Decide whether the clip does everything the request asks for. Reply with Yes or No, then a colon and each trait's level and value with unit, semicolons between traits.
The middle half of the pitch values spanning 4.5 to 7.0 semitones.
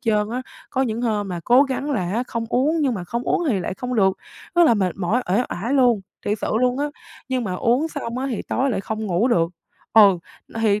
No: average, 4.1 semitones